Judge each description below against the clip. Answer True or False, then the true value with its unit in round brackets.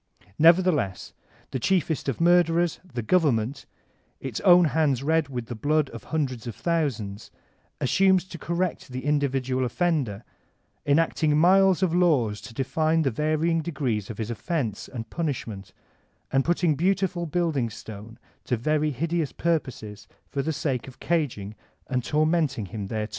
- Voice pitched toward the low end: False (145 Hz)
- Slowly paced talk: False (145 wpm)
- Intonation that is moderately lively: False (5.7 semitones)